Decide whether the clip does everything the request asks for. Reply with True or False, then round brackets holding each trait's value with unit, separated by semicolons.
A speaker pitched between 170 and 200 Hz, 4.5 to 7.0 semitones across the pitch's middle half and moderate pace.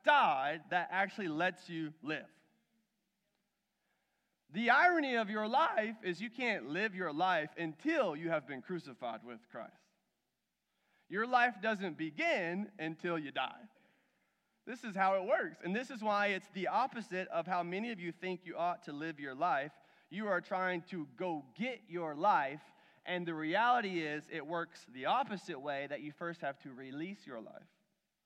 True (185 Hz; 5.1 semitones; 170 wpm)